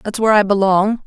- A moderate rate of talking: No, fast, 225 wpm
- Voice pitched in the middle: No, high, 205 Hz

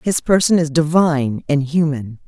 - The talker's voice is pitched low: No, medium, 150 Hz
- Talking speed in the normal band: Yes, average, 160 wpm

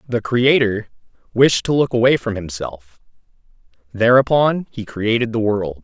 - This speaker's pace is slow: Yes, slow, 125 wpm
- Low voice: Yes, low, 115 Hz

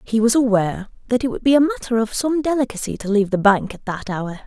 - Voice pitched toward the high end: Yes, high, 230 Hz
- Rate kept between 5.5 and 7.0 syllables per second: Yes, 6.4 syllables/s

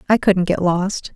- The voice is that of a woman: Yes, female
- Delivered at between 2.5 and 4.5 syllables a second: Yes, 4.1 syllables/s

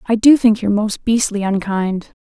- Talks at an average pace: Yes, average, 190 wpm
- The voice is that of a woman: Yes, female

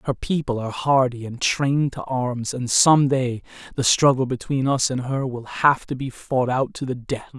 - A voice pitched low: Yes, low, 130 Hz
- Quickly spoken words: Yes, fast, 210 wpm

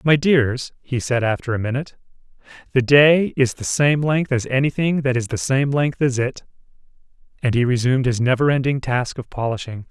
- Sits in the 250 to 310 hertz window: No, low, 130 Hz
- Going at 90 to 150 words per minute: No, average, 190 wpm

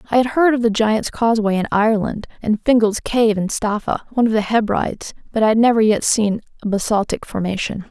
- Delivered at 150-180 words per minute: No, fast, 205 wpm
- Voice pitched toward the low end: No, high, 220 Hz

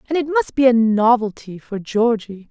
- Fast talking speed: No, average, 190 wpm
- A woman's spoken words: Yes, female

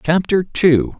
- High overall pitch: No, medium, 165 Hz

